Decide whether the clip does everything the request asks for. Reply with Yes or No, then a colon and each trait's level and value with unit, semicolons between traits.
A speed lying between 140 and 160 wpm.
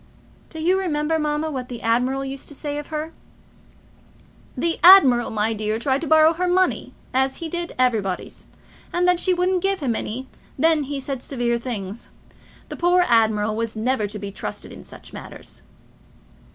No: average, 175 wpm